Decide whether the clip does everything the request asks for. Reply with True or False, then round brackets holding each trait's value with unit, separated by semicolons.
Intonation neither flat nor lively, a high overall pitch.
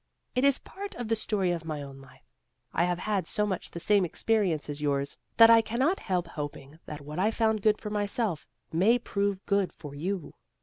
False (6.0 semitones; 195 Hz)